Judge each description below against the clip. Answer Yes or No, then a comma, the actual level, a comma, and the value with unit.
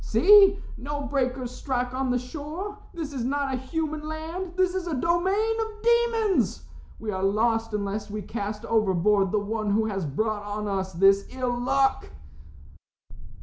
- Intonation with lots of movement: Yes, wide, 7.6 semitones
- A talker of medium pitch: No, very high, 255 Hz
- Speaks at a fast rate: No, average, 160 wpm